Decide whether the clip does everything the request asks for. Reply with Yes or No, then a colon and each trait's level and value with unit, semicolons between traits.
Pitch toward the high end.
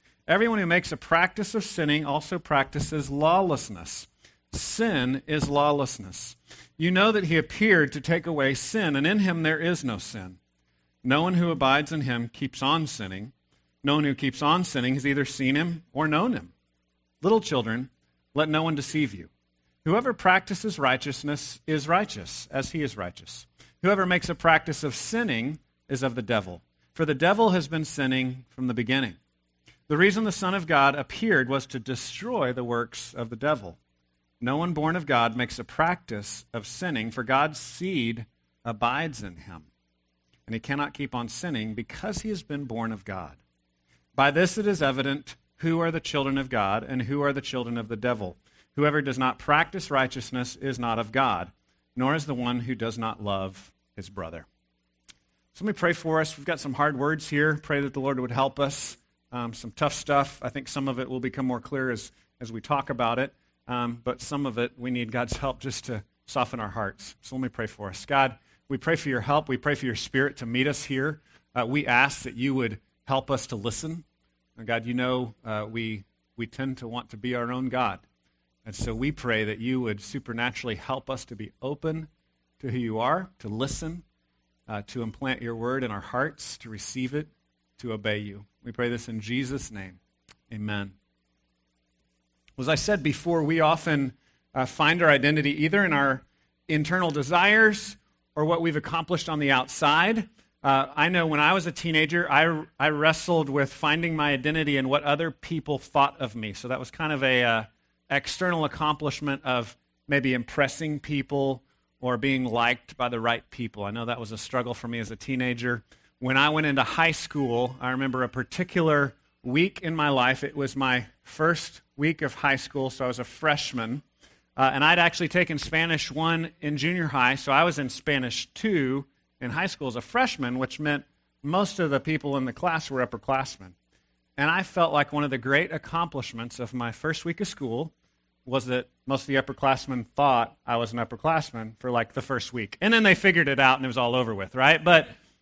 No: low, 135 Hz